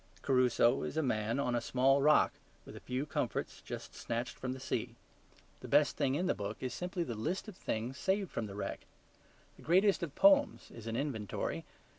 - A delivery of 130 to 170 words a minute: No, average, 200 wpm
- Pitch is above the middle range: No, low, 130 Hz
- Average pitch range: No, wide, 6.2 semitones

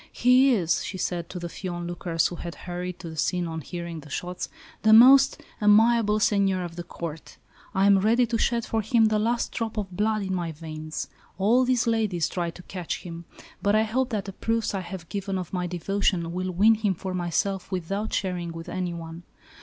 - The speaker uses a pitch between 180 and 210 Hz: Yes, high, 190 Hz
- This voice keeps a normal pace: No, fast, 210 wpm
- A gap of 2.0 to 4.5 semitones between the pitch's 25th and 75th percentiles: Yes, average, 3.8 semitones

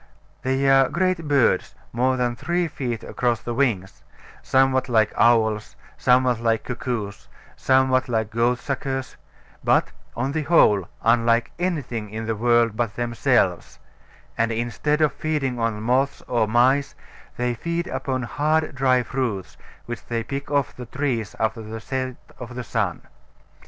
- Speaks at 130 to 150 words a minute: Yes, average, 140 wpm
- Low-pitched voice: Yes, low, 125 Hz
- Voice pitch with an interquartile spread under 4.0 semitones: Yes, average, 2.8 semitones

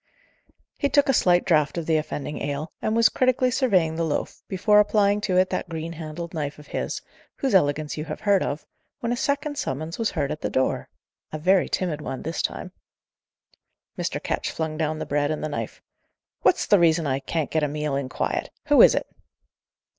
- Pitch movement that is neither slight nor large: Yes, average, 4.9 semitones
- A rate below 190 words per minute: No, fast, 205 wpm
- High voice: No, medium, 160 Hz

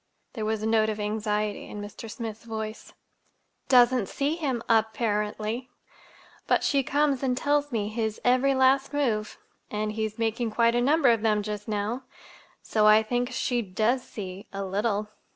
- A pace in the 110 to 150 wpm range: No, average, 160 wpm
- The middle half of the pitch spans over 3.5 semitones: No, average, 2.9 semitones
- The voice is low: No, high, 220 Hz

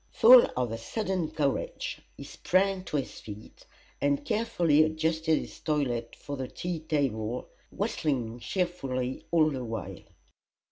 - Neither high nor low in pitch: Yes, medium, 150 Hz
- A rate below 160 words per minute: Yes, slow, 135 wpm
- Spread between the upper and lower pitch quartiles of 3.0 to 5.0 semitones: No, wide, 5.5 semitones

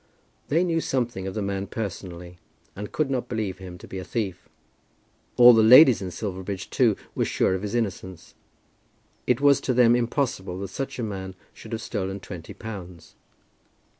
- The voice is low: Yes, low, 105 Hz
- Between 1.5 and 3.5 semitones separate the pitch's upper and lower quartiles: No, average, 4.4 semitones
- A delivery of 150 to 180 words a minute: Yes, average, 175 wpm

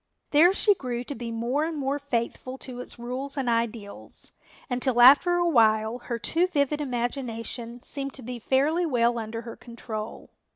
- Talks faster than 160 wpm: Yes, average, 170 wpm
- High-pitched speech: Yes, very high, 250 Hz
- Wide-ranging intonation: No, average, 3.3 semitones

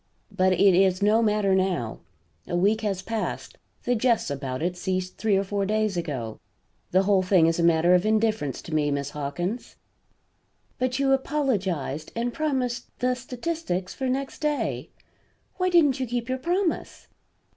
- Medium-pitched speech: No, high, 205 Hz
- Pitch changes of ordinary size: No, wide, 6.2 semitones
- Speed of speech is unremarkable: Yes, average, 165 wpm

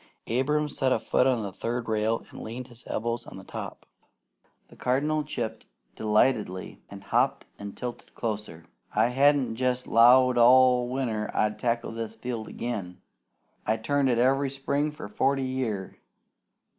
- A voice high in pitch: No, low, 120 Hz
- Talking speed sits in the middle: Yes, average, 155 wpm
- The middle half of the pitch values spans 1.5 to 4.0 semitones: Yes, average, 2.9 semitones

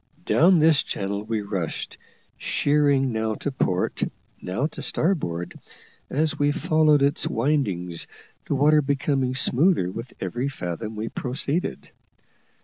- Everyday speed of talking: No, slow, 125 wpm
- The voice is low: Yes, low, 130 Hz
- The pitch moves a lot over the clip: Yes, wide, 5.9 semitones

